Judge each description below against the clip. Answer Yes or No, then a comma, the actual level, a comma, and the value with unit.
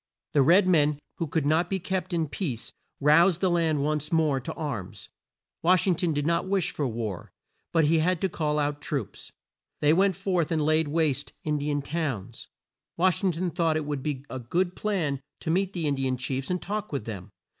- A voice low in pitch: No, medium, 155 Hz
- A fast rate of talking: Yes, fast, 215 wpm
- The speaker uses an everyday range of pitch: Yes, average, 3.6 semitones